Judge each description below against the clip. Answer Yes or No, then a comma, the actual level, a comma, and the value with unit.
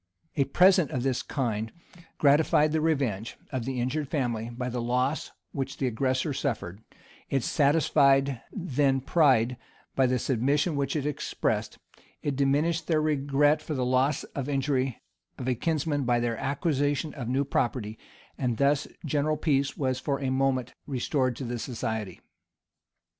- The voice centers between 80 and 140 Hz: Yes, low, 135 Hz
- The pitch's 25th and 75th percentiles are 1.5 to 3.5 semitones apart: Yes, narrow, 2.6 semitones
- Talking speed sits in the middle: Yes, average, 155 wpm